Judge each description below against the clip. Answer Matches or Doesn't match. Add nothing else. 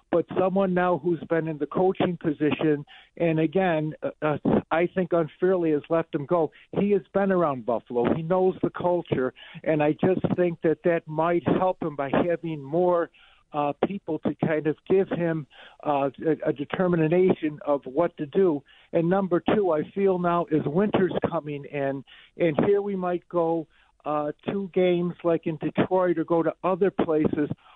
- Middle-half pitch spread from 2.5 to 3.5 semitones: Matches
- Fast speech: Doesn't match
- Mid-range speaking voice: Matches